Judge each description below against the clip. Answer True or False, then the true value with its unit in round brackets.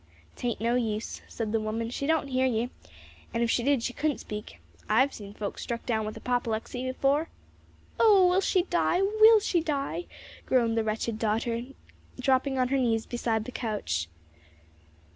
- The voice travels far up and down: False (3.9 semitones)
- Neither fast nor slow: True (170 wpm)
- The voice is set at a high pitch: True (245 Hz)